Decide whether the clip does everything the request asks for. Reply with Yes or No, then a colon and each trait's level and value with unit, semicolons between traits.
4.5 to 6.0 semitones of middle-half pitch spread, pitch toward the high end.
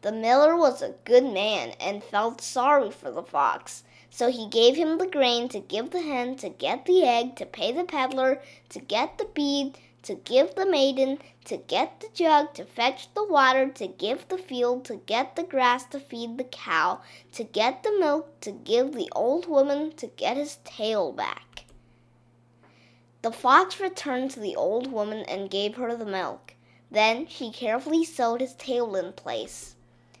Yes: average, 5.1 semitones; very high, 255 Hz